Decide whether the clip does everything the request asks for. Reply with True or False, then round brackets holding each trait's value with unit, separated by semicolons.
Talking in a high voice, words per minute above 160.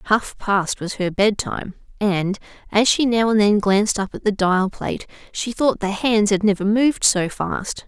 True (205 Hz; 200 wpm)